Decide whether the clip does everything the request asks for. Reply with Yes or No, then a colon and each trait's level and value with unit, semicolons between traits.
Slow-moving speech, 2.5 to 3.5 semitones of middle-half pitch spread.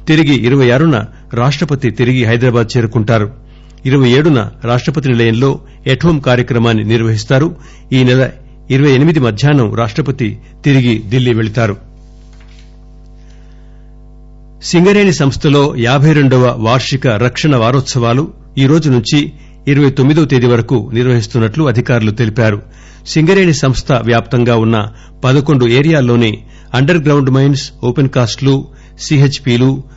Yes: slow, 100 wpm; average, 2.8 semitones